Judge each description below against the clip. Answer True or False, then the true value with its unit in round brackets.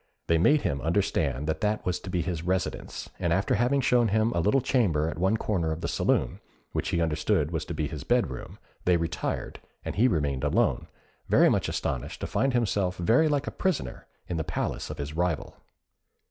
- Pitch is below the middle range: True (85 Hz)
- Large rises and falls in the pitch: True (5.8 semitones)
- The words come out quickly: True (210 wpm)